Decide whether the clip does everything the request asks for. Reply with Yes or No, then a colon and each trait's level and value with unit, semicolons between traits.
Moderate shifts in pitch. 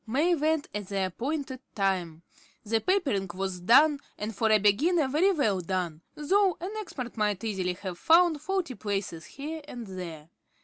No: wide, 8.4 semitones